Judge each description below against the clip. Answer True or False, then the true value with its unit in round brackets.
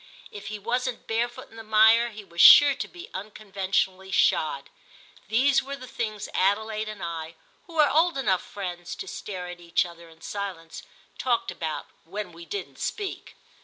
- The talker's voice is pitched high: True (205 Hz)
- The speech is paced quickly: False (170 wpm)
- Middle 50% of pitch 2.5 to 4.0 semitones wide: False (5.0 semitones)